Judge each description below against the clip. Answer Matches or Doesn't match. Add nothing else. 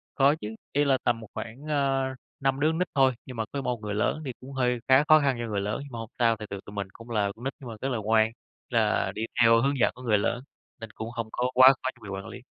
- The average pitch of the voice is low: Matches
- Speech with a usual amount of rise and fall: Matches